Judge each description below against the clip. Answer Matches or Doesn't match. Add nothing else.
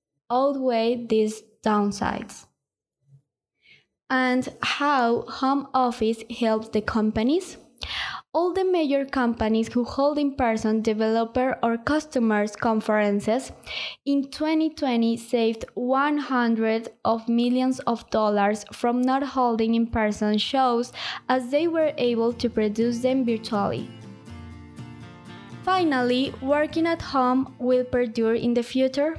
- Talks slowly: Matches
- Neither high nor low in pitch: Doesn't match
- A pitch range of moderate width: Matches